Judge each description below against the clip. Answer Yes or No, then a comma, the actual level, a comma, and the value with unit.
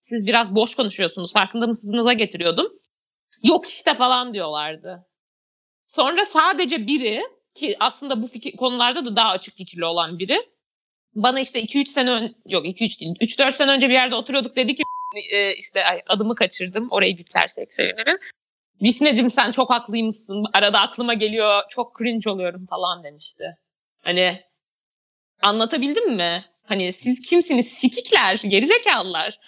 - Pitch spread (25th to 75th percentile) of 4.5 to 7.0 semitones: Yes, average, 5.2 semitones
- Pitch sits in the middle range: No, high, 230 Hz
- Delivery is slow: No, fast, 140 wpm